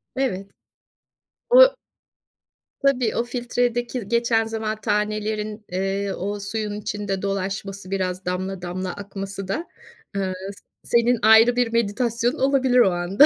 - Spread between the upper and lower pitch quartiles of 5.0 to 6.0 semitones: No, average, 3.5 semitones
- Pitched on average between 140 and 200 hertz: No, high, 210 Hz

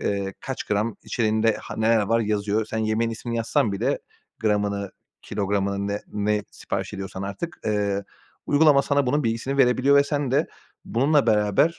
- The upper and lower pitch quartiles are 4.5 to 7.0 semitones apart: No, average, 3.8 semitones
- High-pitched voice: No, low, 110 Hz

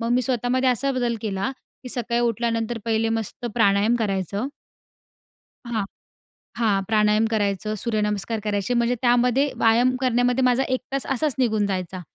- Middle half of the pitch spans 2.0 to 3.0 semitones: Yes, average, 2.7 semitones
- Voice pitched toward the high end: Yes, high, 230 Hz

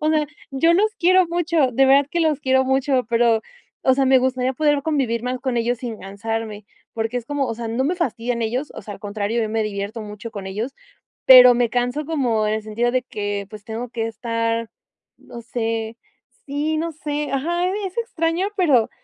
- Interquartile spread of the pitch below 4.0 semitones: No, average, 4.5 semitones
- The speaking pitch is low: No, very high, 250 Hz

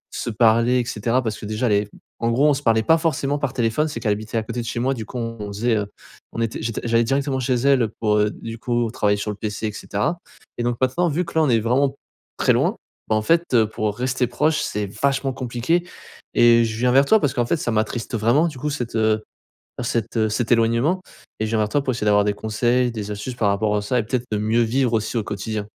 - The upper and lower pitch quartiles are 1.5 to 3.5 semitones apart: Yes, average, 3.2 semitones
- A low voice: Yes, low, 115 Hz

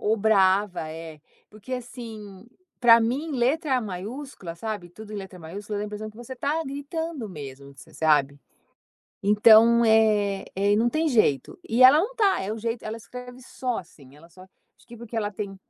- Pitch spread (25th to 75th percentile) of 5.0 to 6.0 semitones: No, average, 4.4 semitones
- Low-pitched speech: No, high, 215 Hz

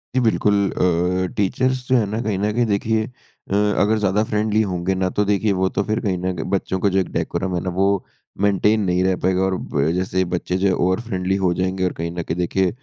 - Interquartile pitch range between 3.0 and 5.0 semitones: No, narrow, 2.4 semitones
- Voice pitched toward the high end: No, very low, 95 Hz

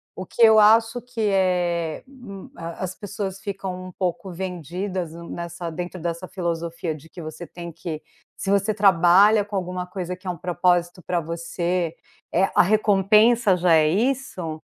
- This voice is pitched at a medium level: Yes, medium, 180 Hz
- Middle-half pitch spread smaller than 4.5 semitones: Yes, average, 2.8 semitones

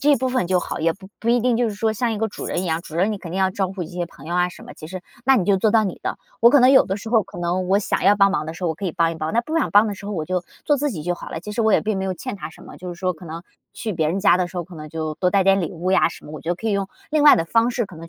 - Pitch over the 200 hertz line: No, high, 190 Hz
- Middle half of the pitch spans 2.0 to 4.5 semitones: Yes, average, 4.2 semitones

